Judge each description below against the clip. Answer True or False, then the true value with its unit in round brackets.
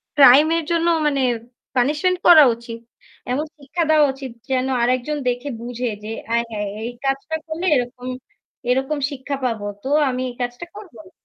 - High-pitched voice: True (265 Hz)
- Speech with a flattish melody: False (3.6 semitones)